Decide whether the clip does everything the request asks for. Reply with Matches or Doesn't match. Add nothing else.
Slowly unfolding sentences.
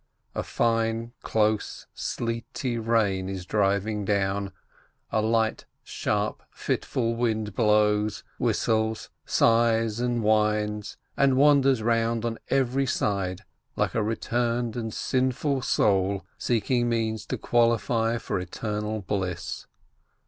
Matches